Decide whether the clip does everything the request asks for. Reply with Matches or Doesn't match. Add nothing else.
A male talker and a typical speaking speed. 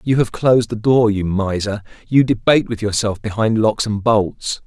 Matches